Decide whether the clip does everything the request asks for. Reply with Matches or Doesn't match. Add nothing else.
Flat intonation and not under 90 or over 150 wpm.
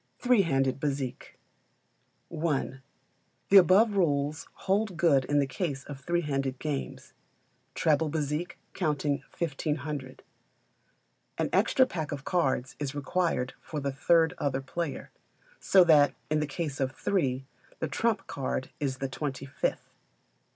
Doesn't match